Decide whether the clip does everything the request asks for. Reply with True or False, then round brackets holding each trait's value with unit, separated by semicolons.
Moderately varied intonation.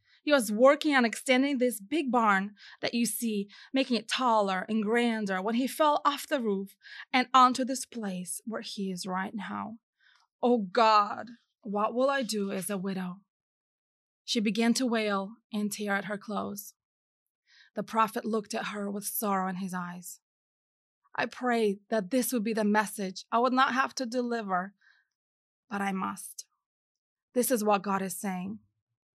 True (4.1 semitones)